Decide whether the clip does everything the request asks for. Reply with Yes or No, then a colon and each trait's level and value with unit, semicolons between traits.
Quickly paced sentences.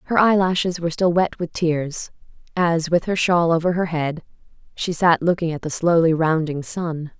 No: average, 185 wpm